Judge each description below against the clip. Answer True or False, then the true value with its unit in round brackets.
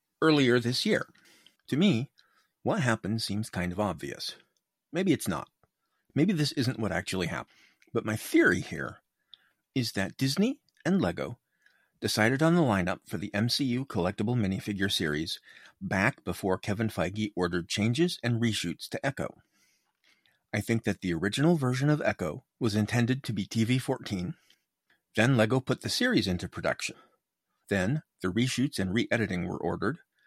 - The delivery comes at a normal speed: True (155 wpm)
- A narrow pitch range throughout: False (5.1 semitones)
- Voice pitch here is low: True (110 Hz)